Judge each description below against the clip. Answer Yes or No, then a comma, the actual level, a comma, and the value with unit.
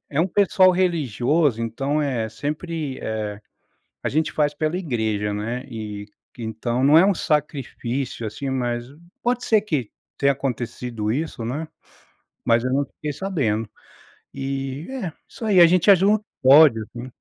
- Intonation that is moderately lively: No, wide, 5.7 semitones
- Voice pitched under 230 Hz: Yes, low, 135 Hz